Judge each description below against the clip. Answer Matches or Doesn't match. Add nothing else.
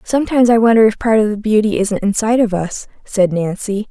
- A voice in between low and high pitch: Doesn't match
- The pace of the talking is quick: Matches